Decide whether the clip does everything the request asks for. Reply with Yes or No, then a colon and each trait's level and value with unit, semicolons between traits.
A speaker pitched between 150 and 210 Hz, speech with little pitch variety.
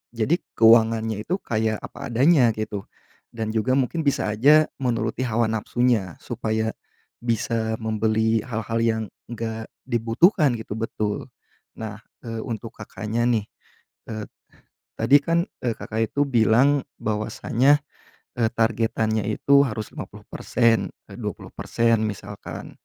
No: low, 115 Hz; narrow, 1.8 semitones